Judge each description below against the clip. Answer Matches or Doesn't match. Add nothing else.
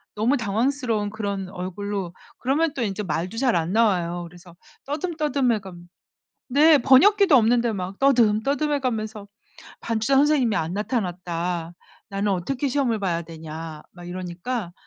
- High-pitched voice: Matches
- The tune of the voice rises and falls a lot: Matches